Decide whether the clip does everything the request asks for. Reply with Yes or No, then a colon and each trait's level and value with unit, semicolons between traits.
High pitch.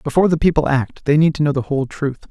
No: medium, 145 Hz